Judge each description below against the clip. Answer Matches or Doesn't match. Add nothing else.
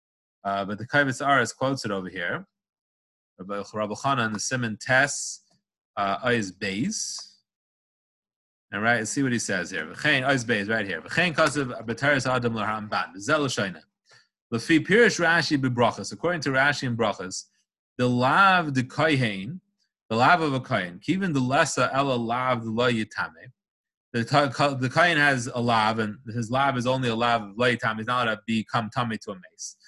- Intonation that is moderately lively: Matches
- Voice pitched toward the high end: Doesn't match